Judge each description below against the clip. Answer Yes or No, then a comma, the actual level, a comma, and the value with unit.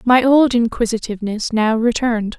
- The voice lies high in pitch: Yes, high, 230 Hz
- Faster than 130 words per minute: No, slow, 125 wpm